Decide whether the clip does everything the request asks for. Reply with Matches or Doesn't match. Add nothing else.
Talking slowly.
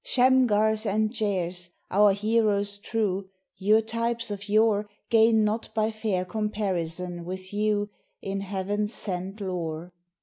Matches